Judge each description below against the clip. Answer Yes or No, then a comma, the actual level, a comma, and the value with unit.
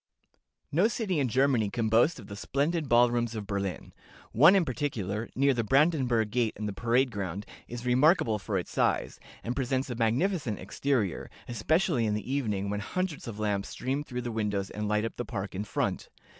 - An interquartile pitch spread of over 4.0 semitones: Yes, average, 4.8 semitones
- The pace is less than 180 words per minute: No, average, 195 wpm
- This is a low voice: Yes, low, 120 Hz